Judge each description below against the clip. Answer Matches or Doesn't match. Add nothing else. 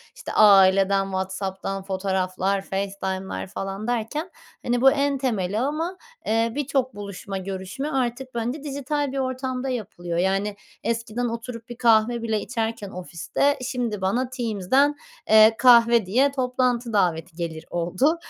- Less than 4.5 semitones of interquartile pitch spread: Doesn't match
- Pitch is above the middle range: Matches